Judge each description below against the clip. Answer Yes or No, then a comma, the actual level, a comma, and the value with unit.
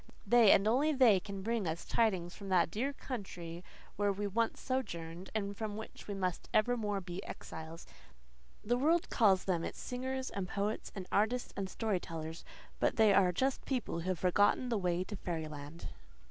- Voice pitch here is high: Yes, high, 200 Hz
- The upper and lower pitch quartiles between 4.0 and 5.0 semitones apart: Yes, average, 4.4 semitones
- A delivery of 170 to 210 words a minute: Yes, average, 185 wpm